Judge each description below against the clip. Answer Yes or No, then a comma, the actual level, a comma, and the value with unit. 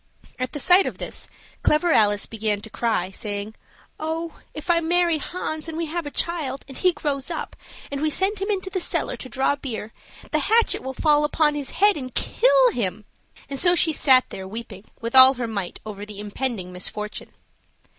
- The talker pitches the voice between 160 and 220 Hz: No, very high, 280 Hz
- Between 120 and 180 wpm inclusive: No, average, 195 wpm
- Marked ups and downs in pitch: Yes, wide, 7.4 semitones